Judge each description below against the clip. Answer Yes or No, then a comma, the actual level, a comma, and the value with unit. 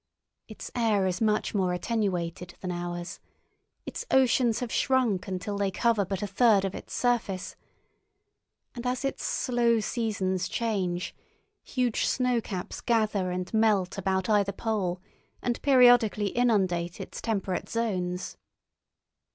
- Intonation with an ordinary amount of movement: Yes, average, 4.0 semitones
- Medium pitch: No, high, 205 Hz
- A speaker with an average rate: No, slow, 125 wpm